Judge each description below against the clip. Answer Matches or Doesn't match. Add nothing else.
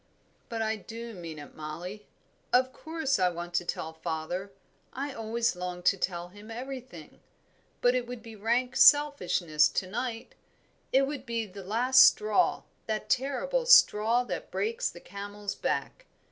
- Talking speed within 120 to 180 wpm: Matches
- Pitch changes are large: Matches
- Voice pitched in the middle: Doesn't match